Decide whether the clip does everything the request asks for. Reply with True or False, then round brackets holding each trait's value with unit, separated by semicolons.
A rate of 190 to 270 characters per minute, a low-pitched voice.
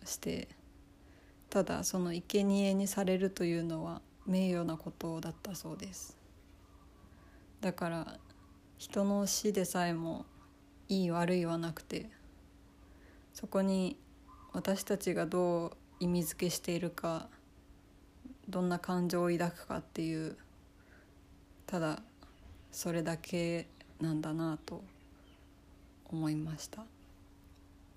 False (205 characters per minute; 165 Hz)